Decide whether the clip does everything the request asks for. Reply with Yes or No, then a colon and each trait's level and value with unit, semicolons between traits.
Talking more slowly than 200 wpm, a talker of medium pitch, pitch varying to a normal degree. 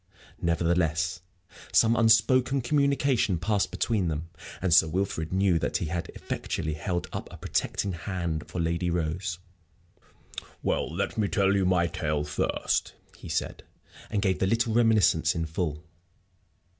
No: average, 145 wpm; very low, 90 Hz; average, 4.3 semitones